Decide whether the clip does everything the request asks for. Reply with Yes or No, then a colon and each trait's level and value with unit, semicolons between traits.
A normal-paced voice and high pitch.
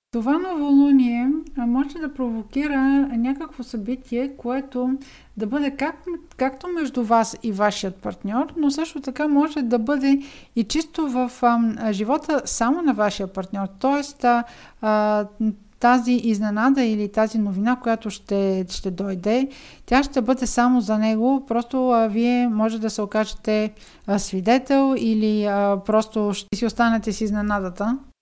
Yes: average, 140 wpm; high, 240 Hz